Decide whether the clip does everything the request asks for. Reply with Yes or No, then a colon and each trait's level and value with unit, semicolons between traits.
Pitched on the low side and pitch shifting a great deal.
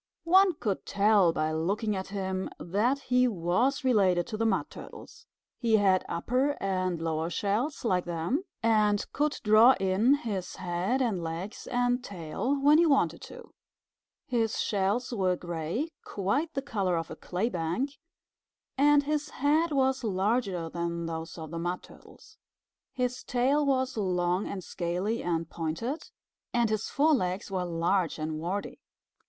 No: high, 205 Hz; wide, 6.4 semitones